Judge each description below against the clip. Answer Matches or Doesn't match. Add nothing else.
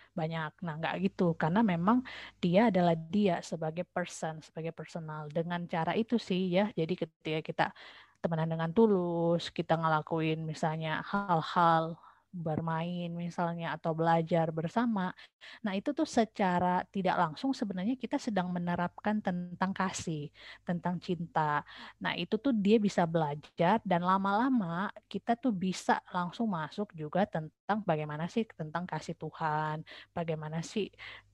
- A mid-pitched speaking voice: Matches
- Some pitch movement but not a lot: Matches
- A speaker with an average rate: Matches